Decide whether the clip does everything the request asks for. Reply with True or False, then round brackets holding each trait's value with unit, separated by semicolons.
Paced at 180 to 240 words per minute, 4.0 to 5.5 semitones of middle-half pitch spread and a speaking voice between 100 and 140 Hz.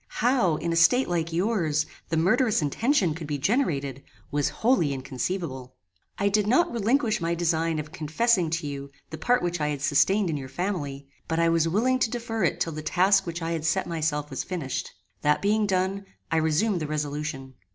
False (195 wpm; 5.2 semitones; 165 Hz)